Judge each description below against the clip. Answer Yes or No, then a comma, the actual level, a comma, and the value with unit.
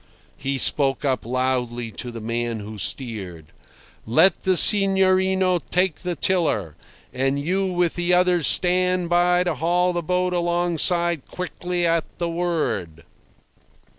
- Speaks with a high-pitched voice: No, medium, 170 Hz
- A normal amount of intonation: No, wide, 5.9 semitones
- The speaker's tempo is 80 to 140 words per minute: Yes, slow, 135 wpm